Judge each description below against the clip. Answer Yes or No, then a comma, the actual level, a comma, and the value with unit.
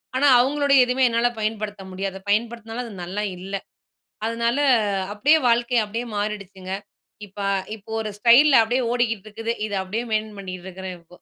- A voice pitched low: No, high, 220 Hz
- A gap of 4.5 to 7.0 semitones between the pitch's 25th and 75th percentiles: No, average, 3.2 semitones